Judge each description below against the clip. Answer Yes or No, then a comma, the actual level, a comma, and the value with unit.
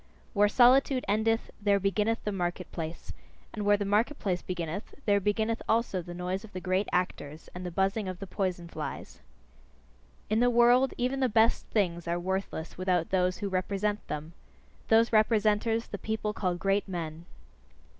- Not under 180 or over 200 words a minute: No, average, 170 wpm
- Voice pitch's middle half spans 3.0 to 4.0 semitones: Yes, average, 3.4 semitones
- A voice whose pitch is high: Yes, high, 200 Hz